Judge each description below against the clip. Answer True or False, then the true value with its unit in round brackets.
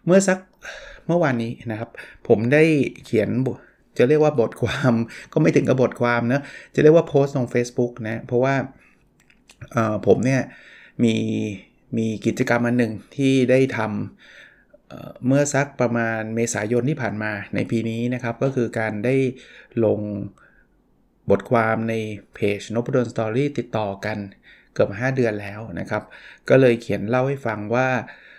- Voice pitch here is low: True (120 Hz)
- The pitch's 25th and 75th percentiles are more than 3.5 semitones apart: False (3.0 semitones)